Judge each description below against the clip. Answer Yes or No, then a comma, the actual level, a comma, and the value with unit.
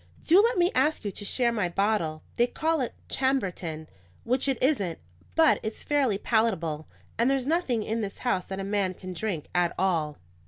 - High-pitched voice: Yes, high, 220 Hz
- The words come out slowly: No, average, 190 wpm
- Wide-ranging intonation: Yes, wide, 6.4 semitones